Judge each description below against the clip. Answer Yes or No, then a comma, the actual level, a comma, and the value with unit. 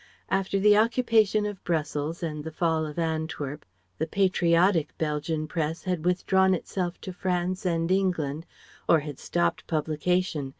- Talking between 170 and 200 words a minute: No, average, 140 wpm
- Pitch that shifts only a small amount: No, average, 3.3 semitones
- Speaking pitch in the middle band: Yes, medium, 170 Hz